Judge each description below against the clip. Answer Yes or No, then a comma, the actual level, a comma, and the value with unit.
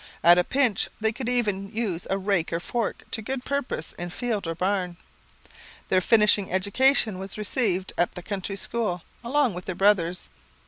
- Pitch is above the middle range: Yes, high, 200 Hz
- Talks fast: No, average, 175 wpm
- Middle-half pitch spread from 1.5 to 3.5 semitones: No, average, 4.3 semitones